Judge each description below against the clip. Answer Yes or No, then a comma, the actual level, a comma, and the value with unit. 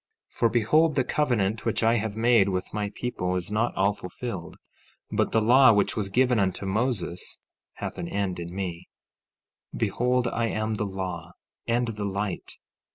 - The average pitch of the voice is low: Yes, low, 105 Hz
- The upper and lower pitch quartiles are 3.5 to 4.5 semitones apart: Yes, average, 3.8 semitones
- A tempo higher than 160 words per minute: Yes, average, 175 wpm